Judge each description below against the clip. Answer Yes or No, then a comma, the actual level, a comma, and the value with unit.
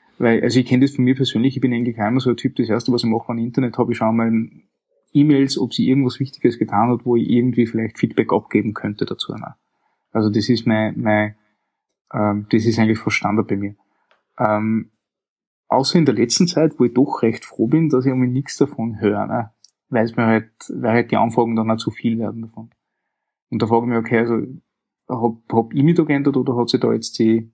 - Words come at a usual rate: No, fast, 230 wpm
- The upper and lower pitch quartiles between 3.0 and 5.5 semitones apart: No, narrow, 2.4 semitones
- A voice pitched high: No, low, 115 Hz